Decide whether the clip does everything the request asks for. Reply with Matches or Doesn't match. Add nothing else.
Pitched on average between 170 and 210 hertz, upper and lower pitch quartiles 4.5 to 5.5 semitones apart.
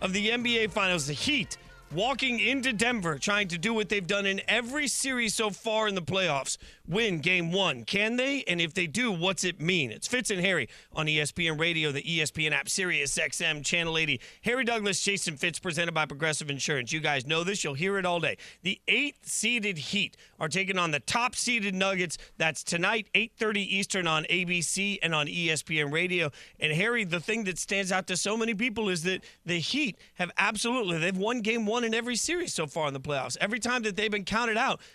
Matches